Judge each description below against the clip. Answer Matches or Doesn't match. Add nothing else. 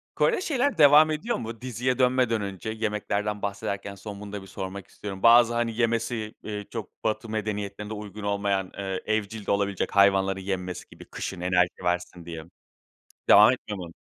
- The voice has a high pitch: Doesn't match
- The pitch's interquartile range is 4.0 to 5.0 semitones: Doesn't match